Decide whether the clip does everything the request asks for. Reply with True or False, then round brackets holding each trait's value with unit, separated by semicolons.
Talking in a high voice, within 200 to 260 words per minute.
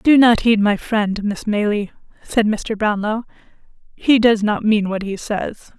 False (215 Hz; 175 wpm)